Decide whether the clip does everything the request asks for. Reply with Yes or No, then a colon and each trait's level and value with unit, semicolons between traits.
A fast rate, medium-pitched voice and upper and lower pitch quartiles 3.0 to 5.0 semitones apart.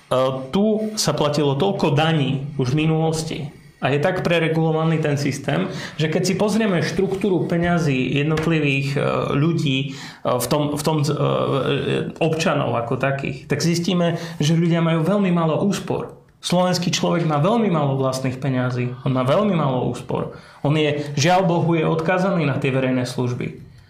No: average, 150 wpm; medium, 155 Hz; average, 3.7 semitones